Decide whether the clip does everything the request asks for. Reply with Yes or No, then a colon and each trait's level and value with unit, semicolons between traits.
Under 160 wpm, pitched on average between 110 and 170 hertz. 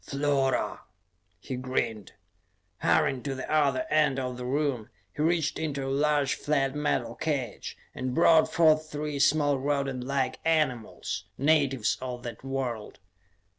Yes: slow, 135 wpm; low, 135 Hz